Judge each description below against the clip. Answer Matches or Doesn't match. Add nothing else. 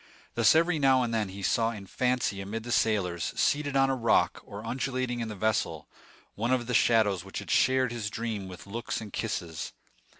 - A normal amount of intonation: Matches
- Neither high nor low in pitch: Doesn't match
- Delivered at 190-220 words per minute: Matches